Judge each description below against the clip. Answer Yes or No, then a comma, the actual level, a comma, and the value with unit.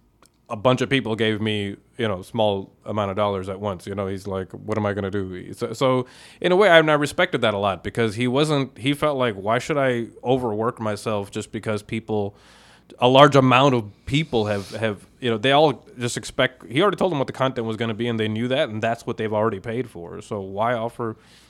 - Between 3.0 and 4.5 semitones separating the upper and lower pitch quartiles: Yes, average, 3.6 semitones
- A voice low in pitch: Yes, low, 115 Hz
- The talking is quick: Yes, fast, 245 wpm